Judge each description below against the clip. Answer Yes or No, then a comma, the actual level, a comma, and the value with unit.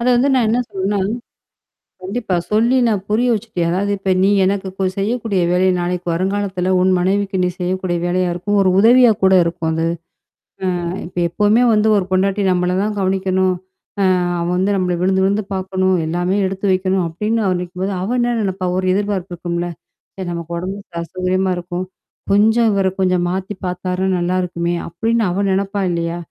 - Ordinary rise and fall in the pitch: No, narrow, 2.1 semitones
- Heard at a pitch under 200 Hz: Yes, high, 190 Hz